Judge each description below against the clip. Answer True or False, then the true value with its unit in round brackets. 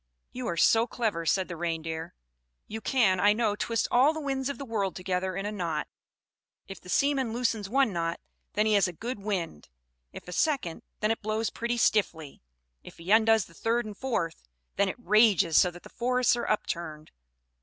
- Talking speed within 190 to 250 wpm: True (195 wpm)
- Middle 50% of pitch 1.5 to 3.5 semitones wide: False (5.0 semitones)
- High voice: True (210 Hz)